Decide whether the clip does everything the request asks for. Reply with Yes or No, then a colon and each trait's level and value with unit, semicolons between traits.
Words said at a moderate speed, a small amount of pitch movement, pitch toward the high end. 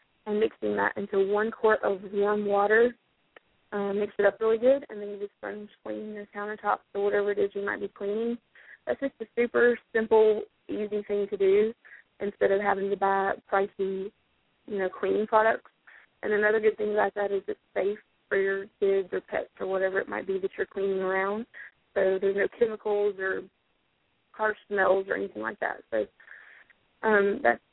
Yes: average, 190 wpm; narrow, 1.8 semitones; high, 205 Hz